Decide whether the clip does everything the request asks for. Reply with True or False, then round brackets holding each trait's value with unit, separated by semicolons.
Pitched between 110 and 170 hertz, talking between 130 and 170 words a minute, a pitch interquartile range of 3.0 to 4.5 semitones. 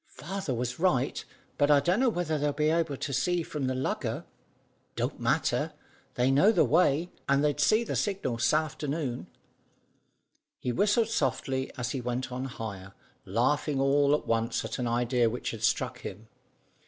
True (140 Hz; 160 wpm; 4.2 semitones)